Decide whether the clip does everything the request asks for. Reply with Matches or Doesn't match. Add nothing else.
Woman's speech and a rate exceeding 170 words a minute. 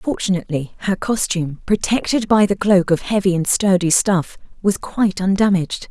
Doesn't match